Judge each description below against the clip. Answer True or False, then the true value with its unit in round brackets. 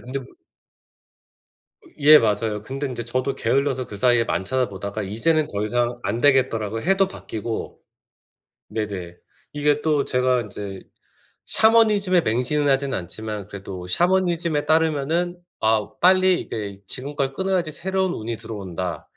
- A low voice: True (130 Hz)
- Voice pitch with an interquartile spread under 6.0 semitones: False (6.6 semitones)